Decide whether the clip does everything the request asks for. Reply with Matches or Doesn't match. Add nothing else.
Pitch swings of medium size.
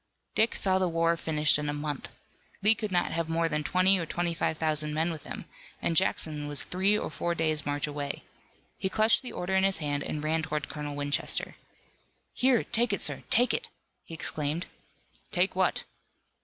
Matches